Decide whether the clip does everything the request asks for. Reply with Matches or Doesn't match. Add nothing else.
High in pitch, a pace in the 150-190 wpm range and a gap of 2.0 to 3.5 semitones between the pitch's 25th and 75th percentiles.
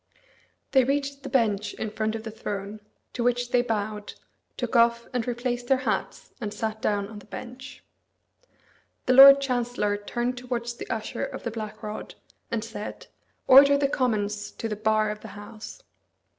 Matches